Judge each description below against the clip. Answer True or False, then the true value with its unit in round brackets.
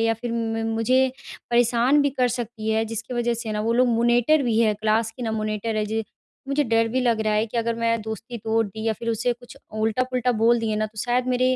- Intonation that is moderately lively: False (1.8 semitones)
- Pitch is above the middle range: True (230 Hz)